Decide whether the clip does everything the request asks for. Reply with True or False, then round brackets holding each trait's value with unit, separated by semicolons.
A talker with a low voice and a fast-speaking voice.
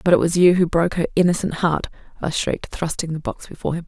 False (170 Hz; 250 wpm)